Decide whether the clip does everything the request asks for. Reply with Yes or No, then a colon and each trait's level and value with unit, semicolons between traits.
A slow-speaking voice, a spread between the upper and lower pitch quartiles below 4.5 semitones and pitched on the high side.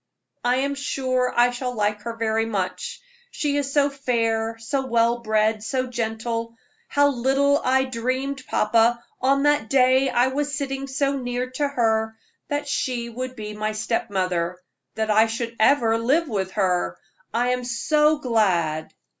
No: average, 160 wpm; average, 3.5 semitones; high, 240 Hz